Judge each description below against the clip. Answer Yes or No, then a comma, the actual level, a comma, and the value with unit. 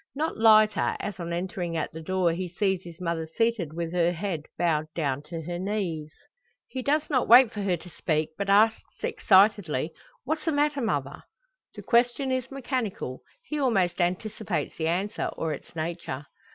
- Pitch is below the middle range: No, medium, 185 Hz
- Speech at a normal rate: Yes, average, 175 wpm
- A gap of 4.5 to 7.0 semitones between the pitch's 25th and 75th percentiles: Yes, average, 5.3 semitones